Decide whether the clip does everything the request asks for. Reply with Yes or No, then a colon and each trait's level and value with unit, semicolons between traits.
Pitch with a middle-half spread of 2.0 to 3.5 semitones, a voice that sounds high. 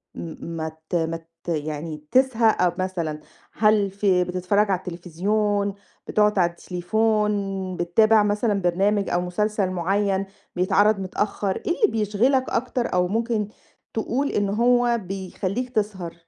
Yes: average, 3.2 semitones; high, 200 Hz